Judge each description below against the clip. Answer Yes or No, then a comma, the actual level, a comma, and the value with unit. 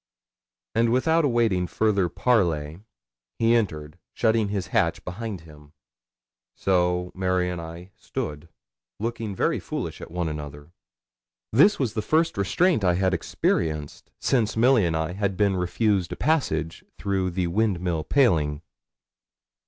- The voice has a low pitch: Yes, very low, 95 Hz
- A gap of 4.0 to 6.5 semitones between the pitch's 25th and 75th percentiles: Yes, average, 5.2 semitones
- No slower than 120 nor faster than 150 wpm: Yes, slow, 135 wpm